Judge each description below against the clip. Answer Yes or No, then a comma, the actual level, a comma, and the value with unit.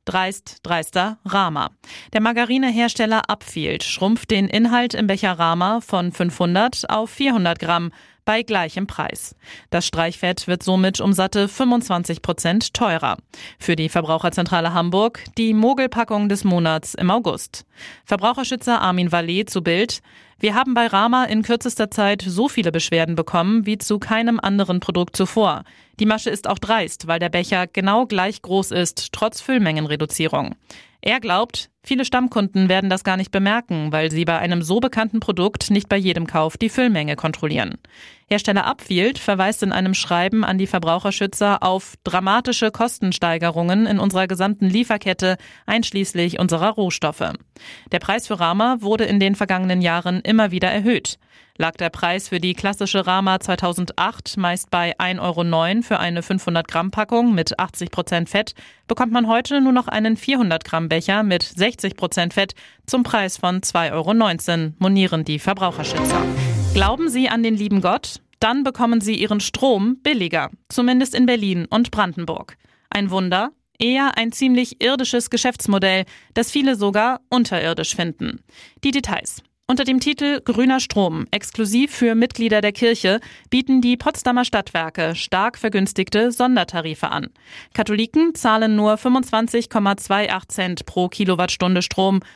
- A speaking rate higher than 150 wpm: No, average, 145 wpm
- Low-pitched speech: No, high, 200 Hz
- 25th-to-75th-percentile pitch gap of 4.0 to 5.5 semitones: Yes, average, 4.4 semitones